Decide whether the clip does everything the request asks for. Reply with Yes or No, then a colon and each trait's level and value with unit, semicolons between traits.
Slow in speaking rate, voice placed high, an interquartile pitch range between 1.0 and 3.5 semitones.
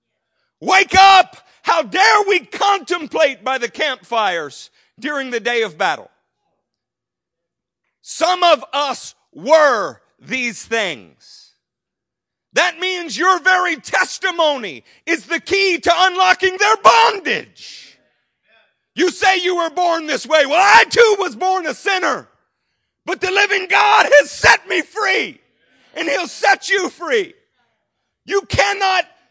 No: slow, 125 wpm; very high, 360 Hz; average, 4.1 semitones